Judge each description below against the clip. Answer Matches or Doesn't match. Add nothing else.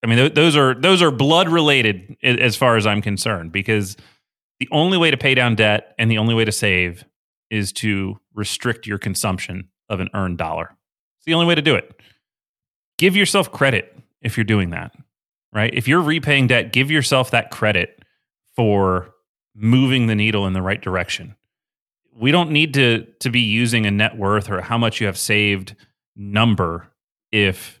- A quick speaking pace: Doesn't match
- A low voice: Matches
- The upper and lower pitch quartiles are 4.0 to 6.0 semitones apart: Matches